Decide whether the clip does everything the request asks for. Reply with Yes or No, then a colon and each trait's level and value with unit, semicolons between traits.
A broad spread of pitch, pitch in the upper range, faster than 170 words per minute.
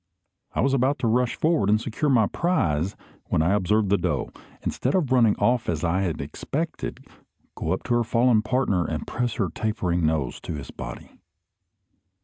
No: wide, 6.2 semitones; low, 110 Hz; average, 180 wpm